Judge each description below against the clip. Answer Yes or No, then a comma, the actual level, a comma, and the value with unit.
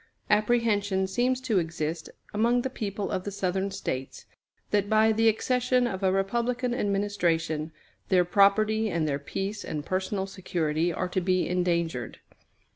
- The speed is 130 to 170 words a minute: Yes, average, 145 wpm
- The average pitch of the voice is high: Yes, high, 195 Hz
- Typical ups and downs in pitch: Yes, average, 3.7 semitones